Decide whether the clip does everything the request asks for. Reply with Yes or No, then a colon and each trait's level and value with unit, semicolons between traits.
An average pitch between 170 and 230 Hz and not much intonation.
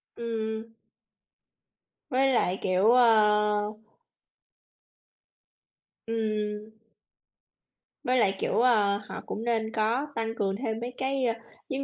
Yes: high, 225 Hz; narrow, 2.2 semitones